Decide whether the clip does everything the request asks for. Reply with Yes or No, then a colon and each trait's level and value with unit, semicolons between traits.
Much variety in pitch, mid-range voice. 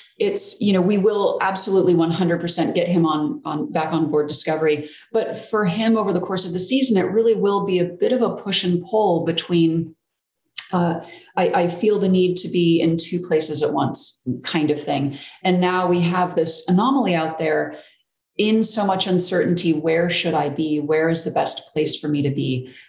No: average, 3.4 semitones; medium, 175 Hz